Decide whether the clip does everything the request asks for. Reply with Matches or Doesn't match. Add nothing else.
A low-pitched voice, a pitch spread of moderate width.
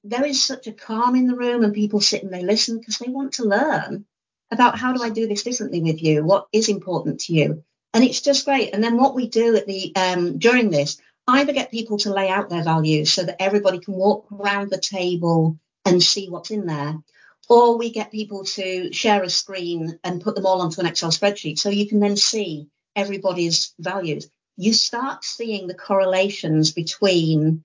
Doesn't match